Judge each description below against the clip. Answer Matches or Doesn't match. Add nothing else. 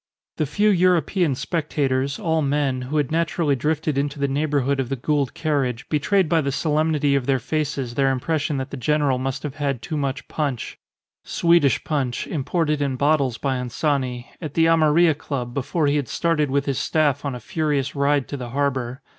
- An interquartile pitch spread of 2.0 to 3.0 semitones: Matches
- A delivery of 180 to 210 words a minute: Matches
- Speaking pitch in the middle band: Matches